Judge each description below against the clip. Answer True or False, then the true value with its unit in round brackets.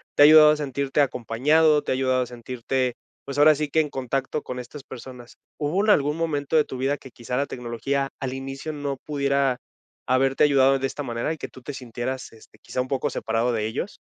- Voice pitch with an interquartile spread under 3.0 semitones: True (2.5 semitones)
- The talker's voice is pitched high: False (135 Hz)